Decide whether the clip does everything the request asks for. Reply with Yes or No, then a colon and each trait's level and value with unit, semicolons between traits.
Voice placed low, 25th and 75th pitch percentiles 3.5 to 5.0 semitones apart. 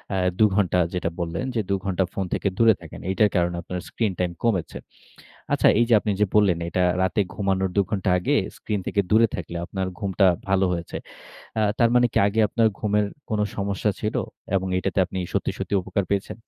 No: very low, 95 Hz; narrow, 2.4 semitones